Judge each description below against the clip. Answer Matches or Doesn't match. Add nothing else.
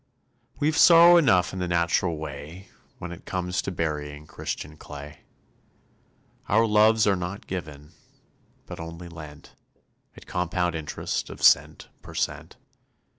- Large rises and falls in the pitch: Doesn't match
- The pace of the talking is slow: Matches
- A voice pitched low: Matches